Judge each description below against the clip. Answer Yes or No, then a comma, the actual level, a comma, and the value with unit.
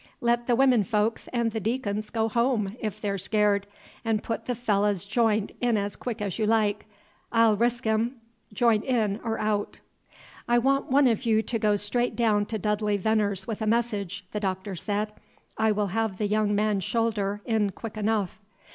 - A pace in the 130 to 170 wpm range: No, average, 190 wpm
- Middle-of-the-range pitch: No, high, 215 Hz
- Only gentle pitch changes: Yes, narrow, 2.0 semitones